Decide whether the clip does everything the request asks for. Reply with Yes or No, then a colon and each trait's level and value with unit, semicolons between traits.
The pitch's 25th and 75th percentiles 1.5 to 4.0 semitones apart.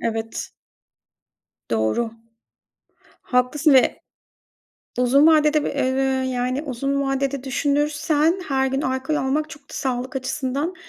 Yes: narrow, 2.4 semitones